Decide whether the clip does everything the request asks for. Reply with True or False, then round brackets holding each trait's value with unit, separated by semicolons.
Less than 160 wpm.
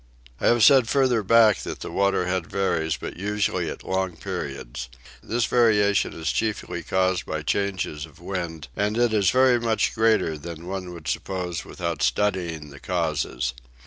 False (165 wpm)